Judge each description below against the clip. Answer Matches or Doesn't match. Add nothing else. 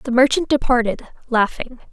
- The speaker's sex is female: Matches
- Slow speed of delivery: Matches